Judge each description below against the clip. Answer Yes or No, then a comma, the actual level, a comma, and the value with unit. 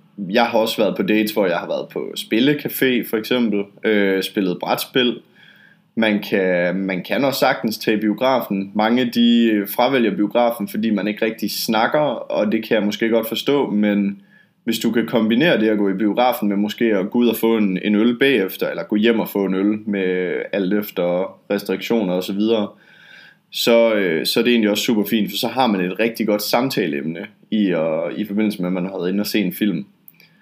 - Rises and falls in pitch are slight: Yes, narrow, 2.3 semitones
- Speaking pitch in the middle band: No, low, 105 Hz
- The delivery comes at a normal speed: Yes, average, 205 wpm